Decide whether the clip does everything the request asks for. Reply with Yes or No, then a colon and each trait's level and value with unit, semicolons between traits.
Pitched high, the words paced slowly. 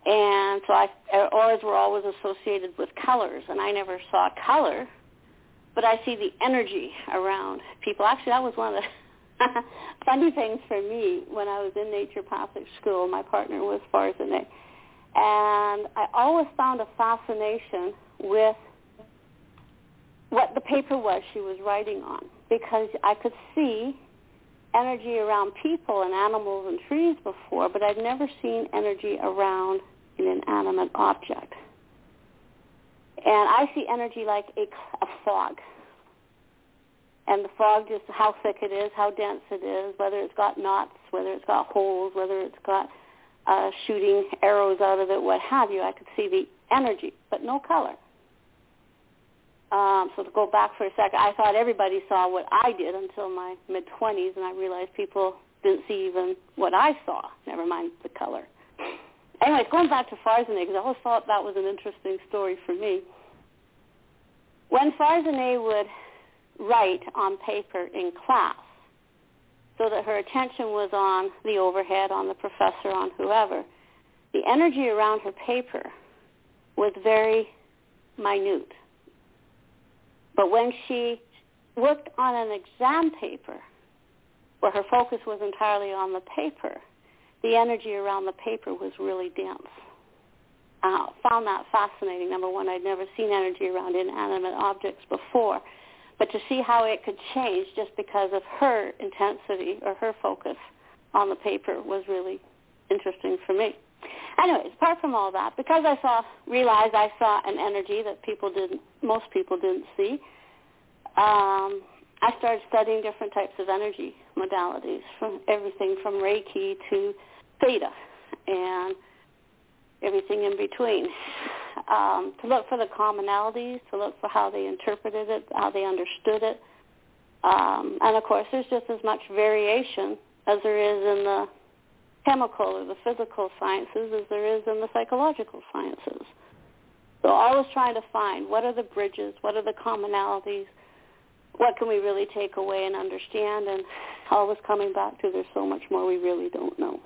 No: high, 215 Hz; average, 155 wpm